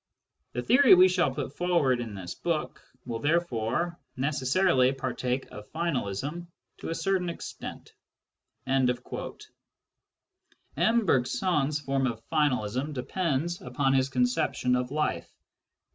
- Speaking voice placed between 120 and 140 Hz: Yes, low, 135 Hz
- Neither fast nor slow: No, slow, 115 wpm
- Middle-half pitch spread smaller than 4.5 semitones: No, wide, 5.4 semitones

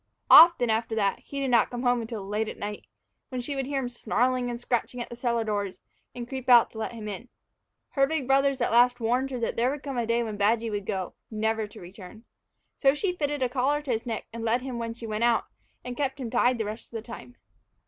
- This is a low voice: No, high, 240 Hz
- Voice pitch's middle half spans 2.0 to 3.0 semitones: Yes, narrow, 2.5 semitones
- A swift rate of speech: Yes, fast, 250 wpm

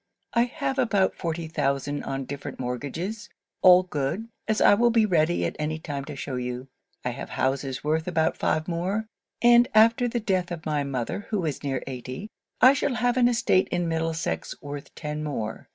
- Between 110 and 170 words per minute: No, average, 185 wpm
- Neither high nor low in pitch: Yes, medium, 165 Hz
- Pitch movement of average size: No, wide, 7.6 semitones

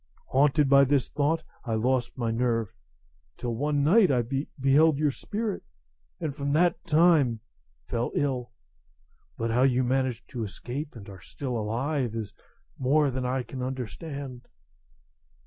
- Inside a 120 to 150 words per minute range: Yes, average, 145 wpm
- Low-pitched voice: Yes, low, 130 Hz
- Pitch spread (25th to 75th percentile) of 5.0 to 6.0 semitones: No, average, 3.2 semitones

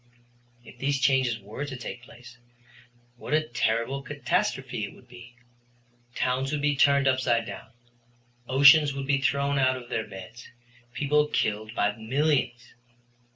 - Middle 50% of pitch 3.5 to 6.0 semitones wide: No, average, 2.9 semitones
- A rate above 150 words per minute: No, average, 145 wpm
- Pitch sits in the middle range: No, low, 130 Hz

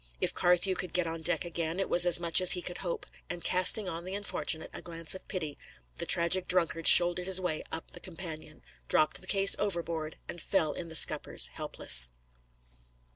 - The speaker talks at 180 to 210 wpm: Yes, average, 195 wpm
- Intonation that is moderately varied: No, narrow, 2.1 semitones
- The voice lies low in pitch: No, medium, 175 Hz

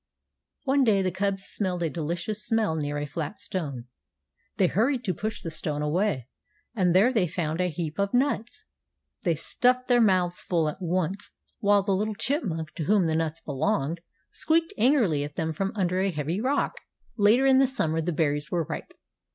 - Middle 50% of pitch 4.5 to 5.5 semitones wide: Yes, average, 5.1 semitones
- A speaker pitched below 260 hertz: Yes, medium, 185 Hz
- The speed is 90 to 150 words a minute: No, average, 185 wpm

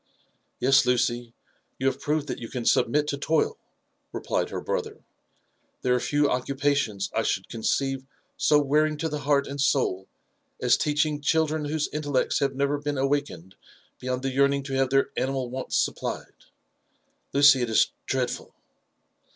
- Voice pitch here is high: No, medium, 140 Hz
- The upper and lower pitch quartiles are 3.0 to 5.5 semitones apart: No, narrow, 2.4 semitones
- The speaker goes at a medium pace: Yes, average, 160 wpm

